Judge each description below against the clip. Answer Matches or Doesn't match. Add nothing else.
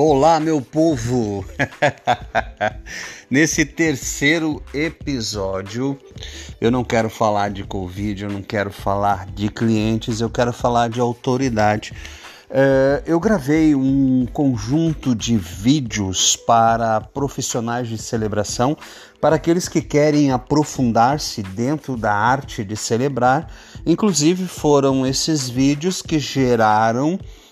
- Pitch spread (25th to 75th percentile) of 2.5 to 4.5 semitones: Doesn't match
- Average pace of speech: Doesn't match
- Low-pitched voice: Matches